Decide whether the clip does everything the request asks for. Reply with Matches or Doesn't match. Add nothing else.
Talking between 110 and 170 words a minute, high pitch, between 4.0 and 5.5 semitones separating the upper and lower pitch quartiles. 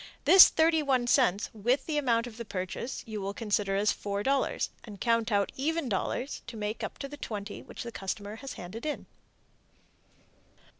Matches